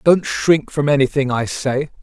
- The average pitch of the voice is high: No, medium, 140 Hz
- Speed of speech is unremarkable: Yes, average, 180 wpm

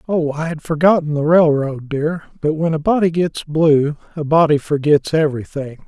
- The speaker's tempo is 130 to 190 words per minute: Yes, average, 175 wpm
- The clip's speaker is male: Yes, male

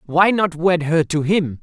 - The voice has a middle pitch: Yes, medium, 165 Hz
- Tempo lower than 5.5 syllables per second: Yes, 4.0 syllables/s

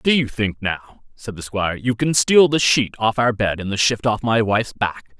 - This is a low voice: Yes, low, 110 Hz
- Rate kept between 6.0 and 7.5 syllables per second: No, 4.8 syllables/s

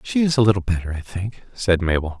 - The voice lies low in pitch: Yes, low, 100 Hz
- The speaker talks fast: Yes, fast, 245 wpm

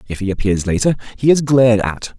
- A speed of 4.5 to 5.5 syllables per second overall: No, 6.0 syllables/s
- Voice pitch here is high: No, low, 115 Hz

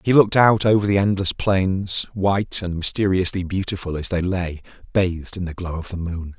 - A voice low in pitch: Yes, very low, 95 Hz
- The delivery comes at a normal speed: Yes, average, 195 wpm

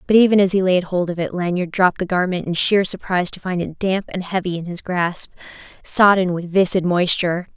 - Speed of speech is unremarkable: No, fast, 220 wpm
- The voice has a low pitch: No, medium, 180 Hz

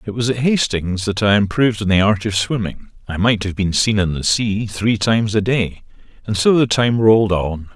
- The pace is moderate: No, fast, 230 wpm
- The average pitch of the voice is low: Yes, low, 105 Hz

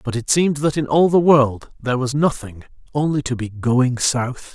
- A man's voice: Yes, male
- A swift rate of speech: Yes, fast, 210 wpm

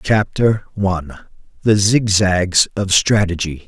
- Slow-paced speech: Yes, slow, 80 wpm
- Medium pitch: No, low, 100 Hz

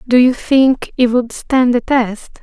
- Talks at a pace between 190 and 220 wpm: Yes, average, 200 wpm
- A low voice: No, very high, 250 Hz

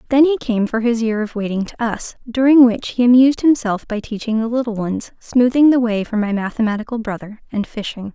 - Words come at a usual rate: No, fast, 215 wpm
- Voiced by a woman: Yes, female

